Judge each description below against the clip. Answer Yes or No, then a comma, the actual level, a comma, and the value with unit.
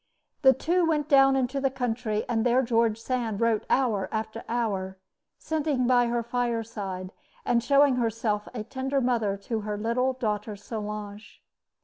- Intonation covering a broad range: No, average, 3.4 semitones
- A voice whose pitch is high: Yes, high, 235 Hz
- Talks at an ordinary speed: Yes, average, 150 wpm